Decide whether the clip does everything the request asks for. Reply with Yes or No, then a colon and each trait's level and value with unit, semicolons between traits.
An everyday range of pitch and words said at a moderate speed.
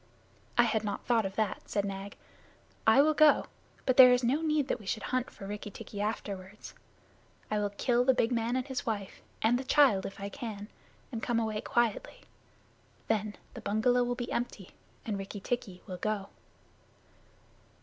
Yes: average, 3.4 semitones; average, 180 wpm